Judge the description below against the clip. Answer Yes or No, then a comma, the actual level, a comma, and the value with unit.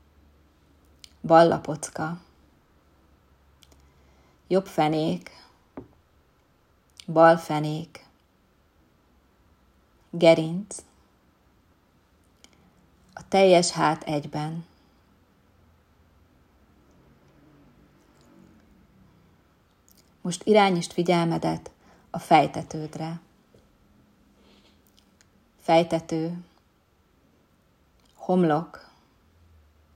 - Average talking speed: No, slow, 35 wpm